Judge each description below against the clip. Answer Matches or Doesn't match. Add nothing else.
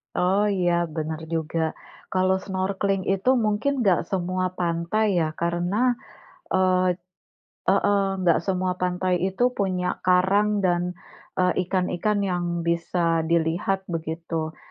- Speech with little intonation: Matches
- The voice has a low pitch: Doesn't match